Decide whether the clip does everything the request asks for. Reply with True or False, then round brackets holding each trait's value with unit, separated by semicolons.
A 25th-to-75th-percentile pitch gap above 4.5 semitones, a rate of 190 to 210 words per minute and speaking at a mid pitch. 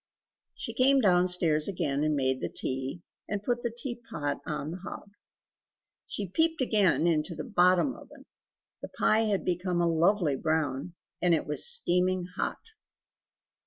False (5.2 semitones; 150 wpm; 180 Hz)